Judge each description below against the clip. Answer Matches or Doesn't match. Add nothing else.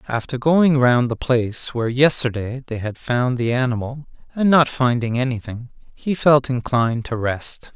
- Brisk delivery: Doesn't match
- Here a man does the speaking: Matches